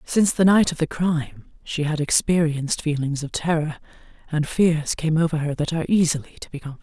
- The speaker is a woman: Yes, female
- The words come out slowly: No, average, 200 wpm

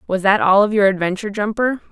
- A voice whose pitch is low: No, high, 205 Hz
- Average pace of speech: No, fast, 220 wpm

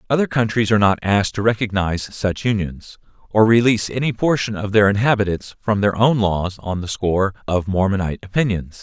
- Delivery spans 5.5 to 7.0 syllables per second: Yes, 5.8 syllables/s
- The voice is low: Yes, low, 105 Hz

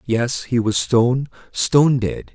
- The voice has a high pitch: No, low, 125 Hz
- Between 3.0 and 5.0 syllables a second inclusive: Yes, 4.0 syllables/s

